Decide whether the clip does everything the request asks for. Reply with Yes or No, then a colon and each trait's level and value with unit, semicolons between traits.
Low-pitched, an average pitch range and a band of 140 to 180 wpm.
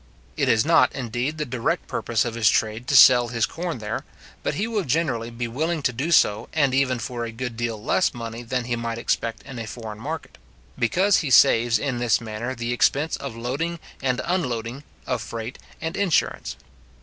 No: low, 120 Hz; average, 3.6 semitones; average, 195 wpm